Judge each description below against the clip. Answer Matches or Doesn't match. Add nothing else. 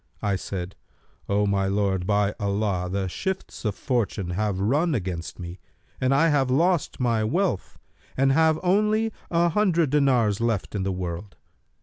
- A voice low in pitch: Matches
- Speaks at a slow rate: Doesn't match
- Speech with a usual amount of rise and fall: Doesn't match